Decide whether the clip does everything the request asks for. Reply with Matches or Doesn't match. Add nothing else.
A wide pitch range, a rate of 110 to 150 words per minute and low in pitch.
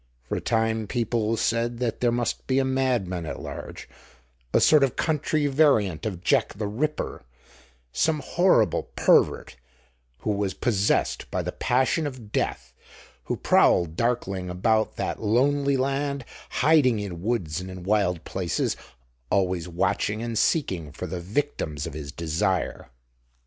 Matches